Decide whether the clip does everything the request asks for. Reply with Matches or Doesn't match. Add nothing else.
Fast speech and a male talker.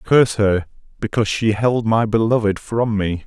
Doesn't match